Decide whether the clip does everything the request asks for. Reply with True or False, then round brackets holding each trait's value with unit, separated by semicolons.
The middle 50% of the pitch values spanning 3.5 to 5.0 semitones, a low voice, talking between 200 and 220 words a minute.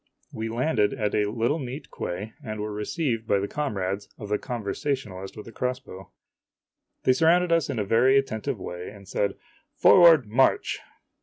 False (4.7 semitones; 115 Hz; 170 wpm)